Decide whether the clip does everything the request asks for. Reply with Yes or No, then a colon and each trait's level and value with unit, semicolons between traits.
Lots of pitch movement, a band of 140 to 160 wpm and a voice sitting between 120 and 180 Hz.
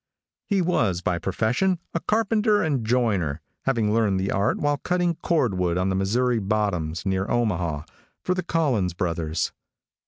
No: wide, 8.2 semitones; average, 150 wpm; low, 110 Hz